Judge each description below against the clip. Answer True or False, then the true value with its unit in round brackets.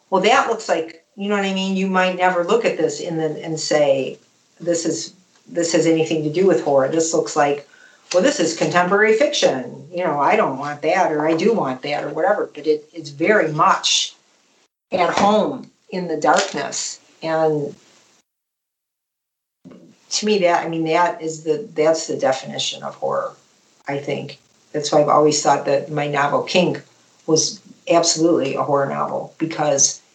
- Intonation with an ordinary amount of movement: True (3.2 semitones)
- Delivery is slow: False (180 wpm)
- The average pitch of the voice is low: False (160 Hz)